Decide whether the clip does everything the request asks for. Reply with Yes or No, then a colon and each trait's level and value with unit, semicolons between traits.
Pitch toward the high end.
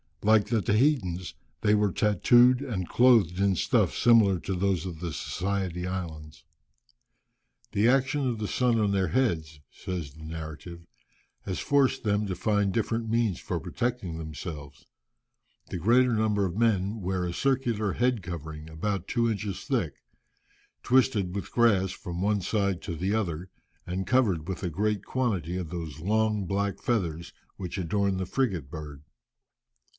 No: low, 100 Hz